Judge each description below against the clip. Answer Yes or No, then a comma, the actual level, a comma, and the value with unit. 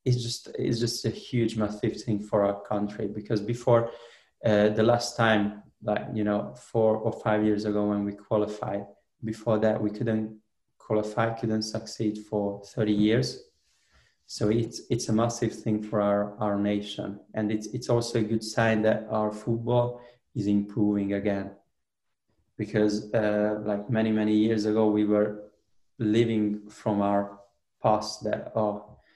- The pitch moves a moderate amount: No, narrow, 1.4 semitones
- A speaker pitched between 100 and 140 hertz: Yes, low, 105 Hz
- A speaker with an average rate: Yes, average, 155 wpm